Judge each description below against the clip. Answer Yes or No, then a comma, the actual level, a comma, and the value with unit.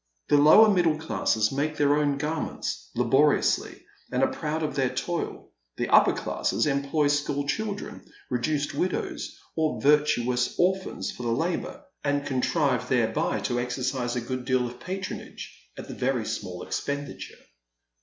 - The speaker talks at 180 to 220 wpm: No, average, 145 wpm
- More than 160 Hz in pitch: No, medium, 145 Hz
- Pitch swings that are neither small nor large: Yes, average, 3.8 semitones